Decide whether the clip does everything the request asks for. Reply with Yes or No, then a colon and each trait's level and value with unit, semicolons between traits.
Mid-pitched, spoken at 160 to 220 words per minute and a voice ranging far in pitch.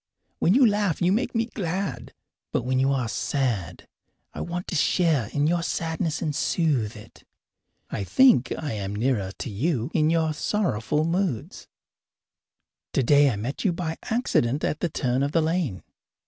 Yes: medium, 150 Hz; average, 165 wpm; wide, 6.0 semitones